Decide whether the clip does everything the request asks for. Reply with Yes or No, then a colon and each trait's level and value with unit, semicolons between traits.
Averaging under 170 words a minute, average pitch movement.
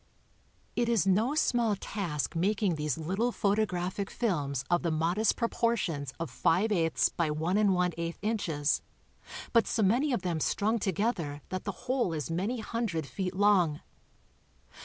Yes: average, 155 wpm; average, 5.0 semitones